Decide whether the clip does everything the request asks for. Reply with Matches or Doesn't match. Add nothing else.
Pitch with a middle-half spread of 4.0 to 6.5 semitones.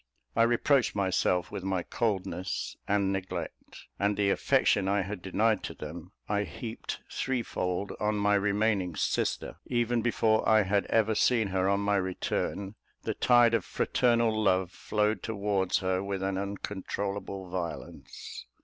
Doesn't match